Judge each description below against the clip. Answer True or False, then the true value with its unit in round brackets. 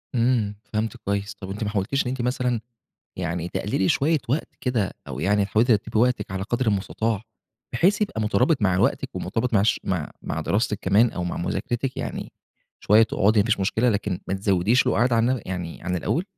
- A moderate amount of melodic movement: True (4.0 semitones)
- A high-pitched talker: False (105 Hz)